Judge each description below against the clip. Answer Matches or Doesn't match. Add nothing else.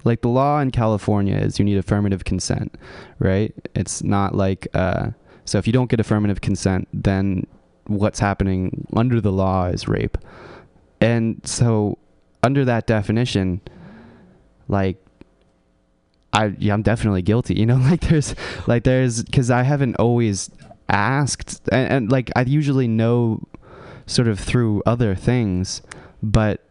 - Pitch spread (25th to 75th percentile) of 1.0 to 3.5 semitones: Doesn't match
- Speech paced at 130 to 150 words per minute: Matches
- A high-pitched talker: Doesn't match